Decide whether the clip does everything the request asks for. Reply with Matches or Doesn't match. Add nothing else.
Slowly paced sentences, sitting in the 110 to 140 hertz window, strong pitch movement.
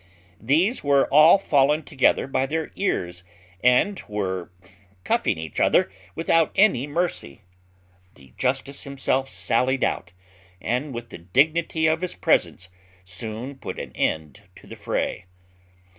Matches